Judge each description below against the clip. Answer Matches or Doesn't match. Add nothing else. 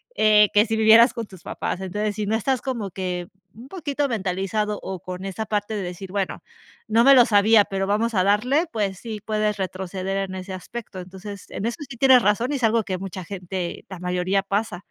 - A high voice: Matches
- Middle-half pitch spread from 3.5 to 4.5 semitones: Doesn't match